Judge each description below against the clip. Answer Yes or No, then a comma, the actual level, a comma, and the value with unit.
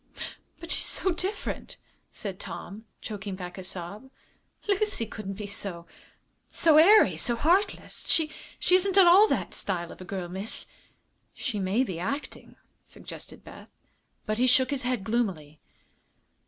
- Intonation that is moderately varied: No, wide, 8.9 semitones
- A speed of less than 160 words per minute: Yes, average, 145 wpm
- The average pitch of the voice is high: Yes, high, 220 Hz